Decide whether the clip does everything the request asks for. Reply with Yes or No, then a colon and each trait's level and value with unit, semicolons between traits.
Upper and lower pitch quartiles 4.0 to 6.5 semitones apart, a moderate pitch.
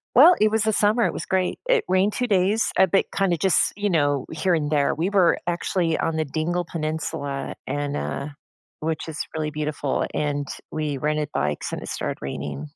Yes: average, 4.5 semitones; medium, 160 Hz